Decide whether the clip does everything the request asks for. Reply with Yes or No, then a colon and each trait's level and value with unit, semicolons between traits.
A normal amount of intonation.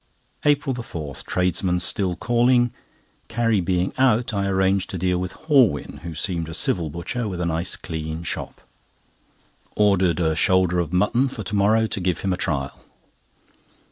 Yes: average, 4.4 semitones